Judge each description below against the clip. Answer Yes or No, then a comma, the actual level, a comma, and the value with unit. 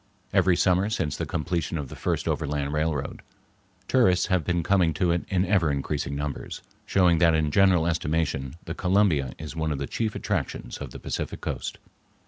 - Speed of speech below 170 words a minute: No, average, 180 wpm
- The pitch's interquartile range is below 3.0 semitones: No, average, 3.7 semitones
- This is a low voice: Yes, very low, 85 Hz